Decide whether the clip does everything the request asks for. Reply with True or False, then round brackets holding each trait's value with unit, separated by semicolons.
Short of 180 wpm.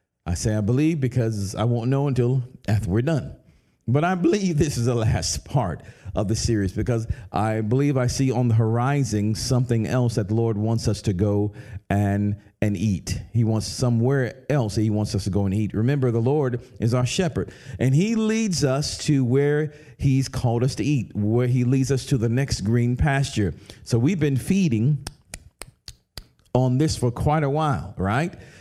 False (195 wpm)